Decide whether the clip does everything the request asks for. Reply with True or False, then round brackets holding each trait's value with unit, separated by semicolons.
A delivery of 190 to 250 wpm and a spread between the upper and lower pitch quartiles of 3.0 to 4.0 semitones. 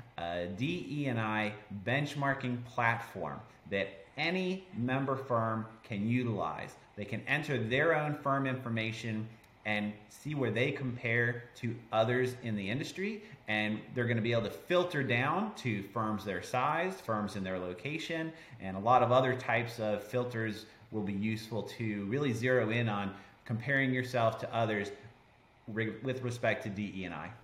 False (150 wpm; 3.4 semitones)